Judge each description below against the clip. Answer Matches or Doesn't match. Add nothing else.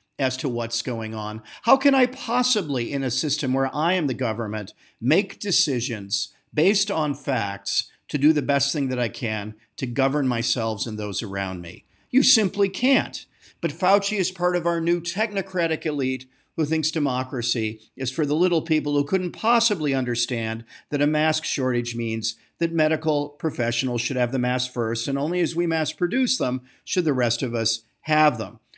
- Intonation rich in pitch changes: Matches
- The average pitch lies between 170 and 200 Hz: Doesn't match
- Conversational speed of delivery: Matches